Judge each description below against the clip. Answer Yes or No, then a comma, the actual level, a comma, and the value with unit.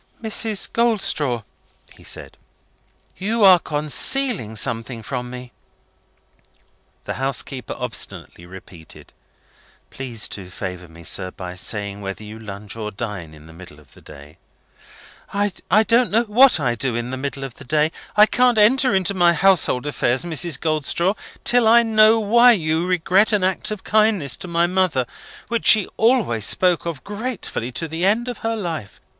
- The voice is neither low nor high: Yes, medium, 160 Hz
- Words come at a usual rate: Yes, average, 160 wpm